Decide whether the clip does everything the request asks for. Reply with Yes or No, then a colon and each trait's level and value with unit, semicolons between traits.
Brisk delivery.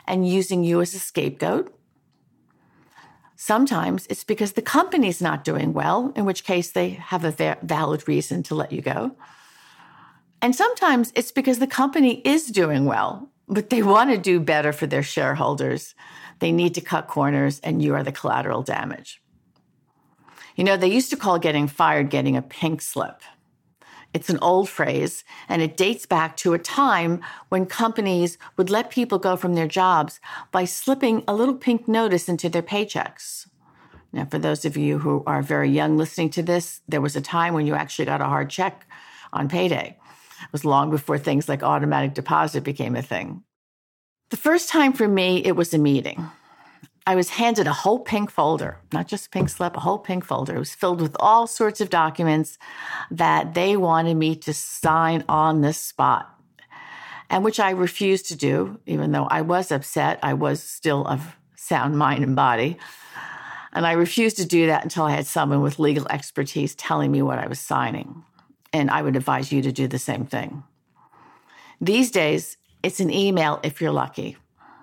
No: average, 185 wpm